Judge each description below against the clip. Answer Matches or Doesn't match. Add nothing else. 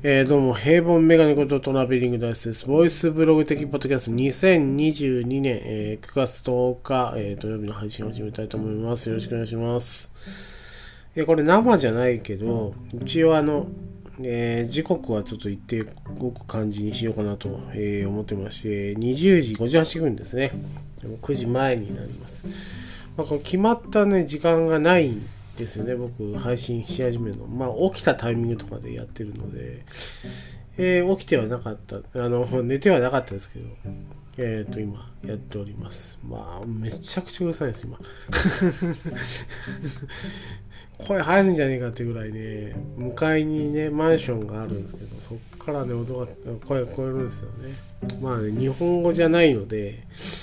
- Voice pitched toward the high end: Doesn't match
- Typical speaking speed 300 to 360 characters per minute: Matches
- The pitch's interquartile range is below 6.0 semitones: Matches